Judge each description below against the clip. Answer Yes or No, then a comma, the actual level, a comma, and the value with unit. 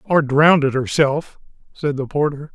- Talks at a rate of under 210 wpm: Yes, average, 140 wpm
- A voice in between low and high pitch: Yes, medium, 145 Hz